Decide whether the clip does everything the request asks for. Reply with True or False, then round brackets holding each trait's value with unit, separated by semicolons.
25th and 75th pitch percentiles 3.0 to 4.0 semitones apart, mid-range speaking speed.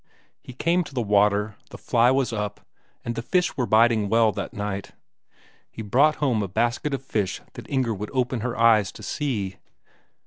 True (3.7 semitones; 185 wpm)